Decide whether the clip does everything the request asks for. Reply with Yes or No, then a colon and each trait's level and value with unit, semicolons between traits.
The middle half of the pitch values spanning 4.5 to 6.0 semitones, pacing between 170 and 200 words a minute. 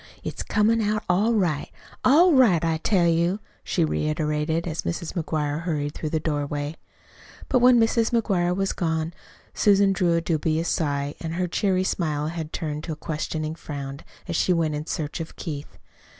No: average, 3.6 semitones; average, 175 wpm